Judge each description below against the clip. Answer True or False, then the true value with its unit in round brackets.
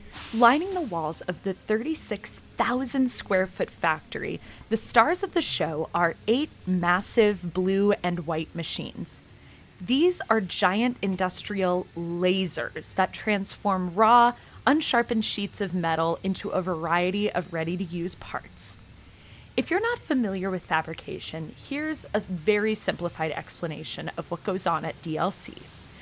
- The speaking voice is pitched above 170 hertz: True (190 Hz)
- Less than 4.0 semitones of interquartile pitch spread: False (5.0 semitones)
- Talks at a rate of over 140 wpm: False (135 wpm)